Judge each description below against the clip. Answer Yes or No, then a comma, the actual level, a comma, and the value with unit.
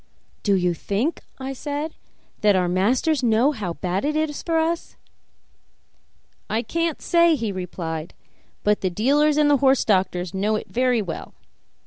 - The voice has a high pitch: Yes, high, 230 Hz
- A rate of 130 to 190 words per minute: Yes, average, 155 wpm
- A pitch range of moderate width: No, wide, 7.7 semitones